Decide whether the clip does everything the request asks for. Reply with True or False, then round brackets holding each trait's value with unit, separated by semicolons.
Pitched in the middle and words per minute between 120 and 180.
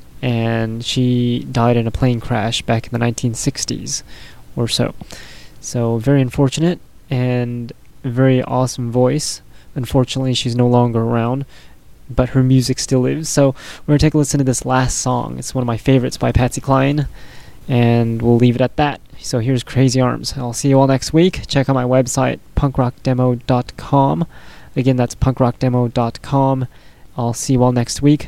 False (130 Hz; 170 wpm)